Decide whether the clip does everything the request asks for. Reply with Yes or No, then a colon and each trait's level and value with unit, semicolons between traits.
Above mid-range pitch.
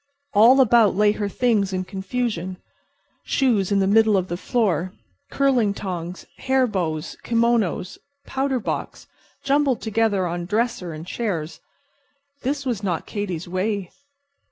Yes: high, 205 Hz